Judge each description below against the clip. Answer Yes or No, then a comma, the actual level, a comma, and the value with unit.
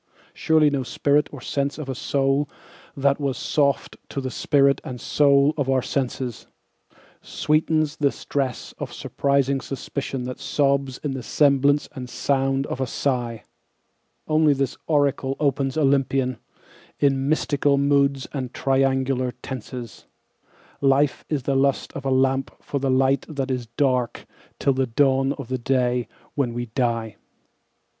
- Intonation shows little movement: Yes, narrow, 1.4 semitones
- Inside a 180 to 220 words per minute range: No, average, 145 wpm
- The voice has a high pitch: No, low, 135 Hz